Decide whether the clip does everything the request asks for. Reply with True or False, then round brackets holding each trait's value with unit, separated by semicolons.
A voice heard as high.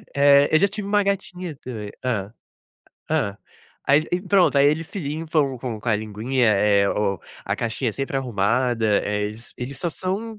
False (130 Hz)